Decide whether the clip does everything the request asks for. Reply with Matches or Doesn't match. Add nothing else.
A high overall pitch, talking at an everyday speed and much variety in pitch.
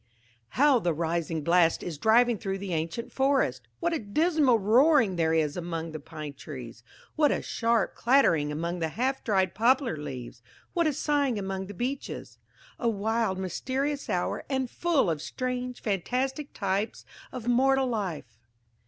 Matches